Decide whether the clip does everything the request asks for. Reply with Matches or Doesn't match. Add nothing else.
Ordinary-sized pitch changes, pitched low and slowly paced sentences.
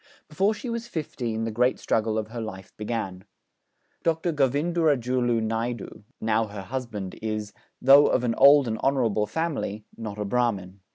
Doesn't match